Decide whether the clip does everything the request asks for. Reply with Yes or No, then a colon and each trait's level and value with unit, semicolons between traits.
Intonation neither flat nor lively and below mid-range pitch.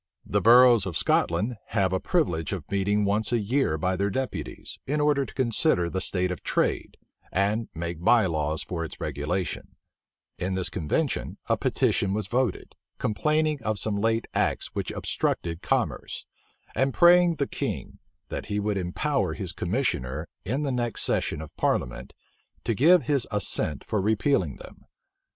No: wide, 6.3 semitones; low, 105 Hz